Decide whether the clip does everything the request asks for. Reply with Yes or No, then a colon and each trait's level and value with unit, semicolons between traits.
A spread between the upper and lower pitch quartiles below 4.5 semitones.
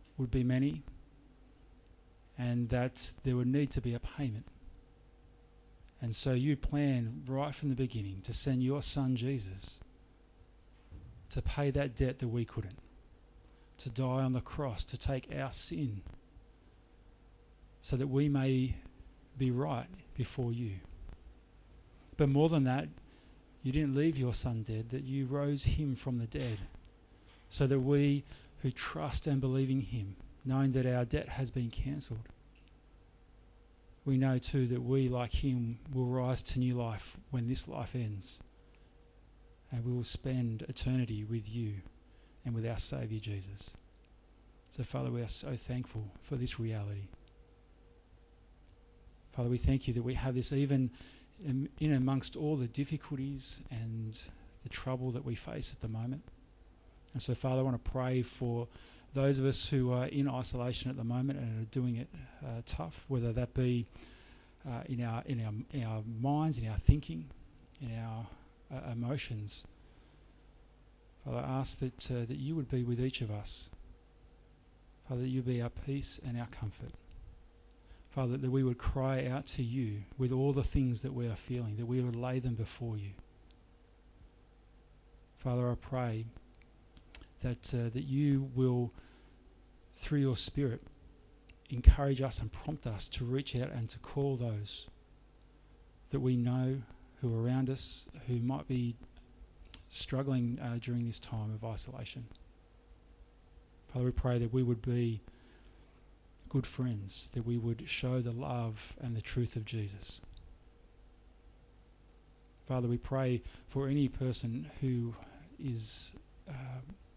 Yes: average, 3.4 semitones